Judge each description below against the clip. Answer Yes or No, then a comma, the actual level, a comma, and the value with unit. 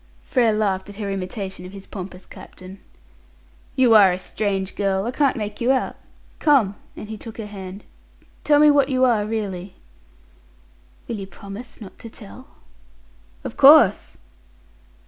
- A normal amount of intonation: Yes, average, 3.8 semitones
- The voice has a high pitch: Yes, high, 210 Hz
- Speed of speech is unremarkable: Yes, average, 155 wpm